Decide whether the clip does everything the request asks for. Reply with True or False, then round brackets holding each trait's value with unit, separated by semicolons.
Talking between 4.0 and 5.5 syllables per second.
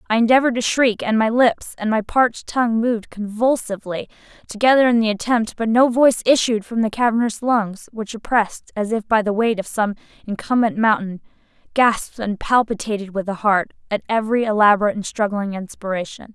False (5.8 syllables/s)